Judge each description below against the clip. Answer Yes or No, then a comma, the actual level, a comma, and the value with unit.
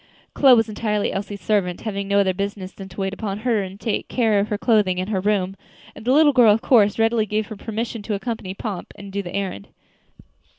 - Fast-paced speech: Yes, fast, 225 wpm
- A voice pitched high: Yes, high, 205 Hz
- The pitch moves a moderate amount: No, narrow, 2.3 semitones